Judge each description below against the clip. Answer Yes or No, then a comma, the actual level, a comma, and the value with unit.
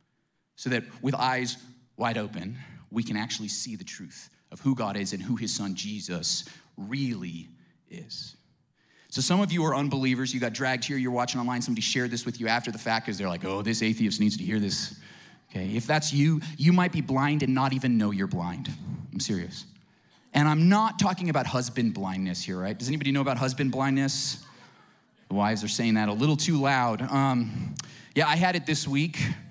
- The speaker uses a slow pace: No, fast, 205 wpm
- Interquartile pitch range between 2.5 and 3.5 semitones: No, average, 4.2 semitones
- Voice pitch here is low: Yes, low, 125 Hz